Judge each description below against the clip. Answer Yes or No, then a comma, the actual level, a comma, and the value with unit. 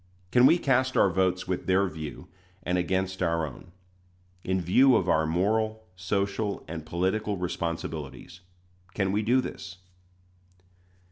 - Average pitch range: Yes, average, 3.4 semitones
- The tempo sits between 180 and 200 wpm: No, slow, 135 wpm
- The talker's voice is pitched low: Yes, very low, 95 Hz